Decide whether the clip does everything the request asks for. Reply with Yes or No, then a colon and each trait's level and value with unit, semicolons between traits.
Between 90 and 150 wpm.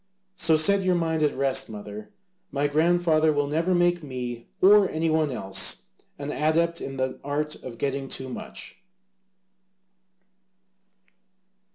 Yes: slow, 135 wpm